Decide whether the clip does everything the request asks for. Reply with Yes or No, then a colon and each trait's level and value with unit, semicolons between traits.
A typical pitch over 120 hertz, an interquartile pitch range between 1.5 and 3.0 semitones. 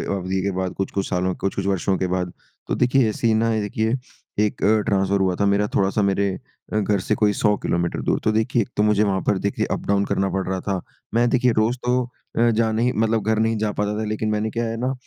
No: low, 105 Hz; narrow, 2.4 semitones